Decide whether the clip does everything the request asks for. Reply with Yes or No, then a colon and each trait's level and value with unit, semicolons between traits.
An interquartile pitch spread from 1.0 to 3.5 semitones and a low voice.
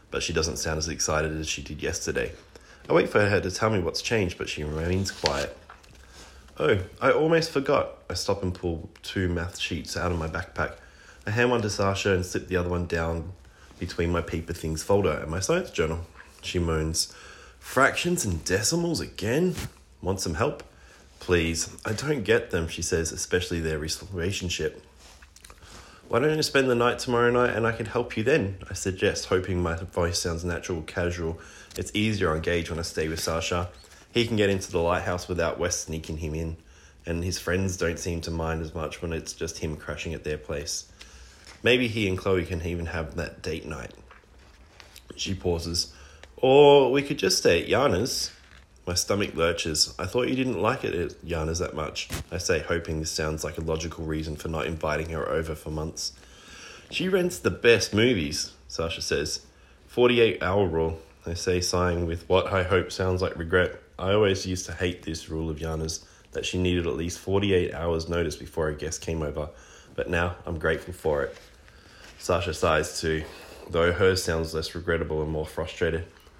Yes: average, 3.0 semitones; very low, 85 Hz